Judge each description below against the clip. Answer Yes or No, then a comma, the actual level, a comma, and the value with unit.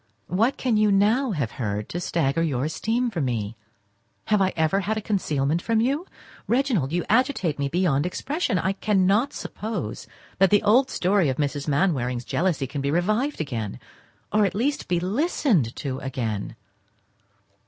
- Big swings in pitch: Yes, wide, 7.6 semitones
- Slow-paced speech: No, average, 165 wpm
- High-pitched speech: No, medium, 180 Hz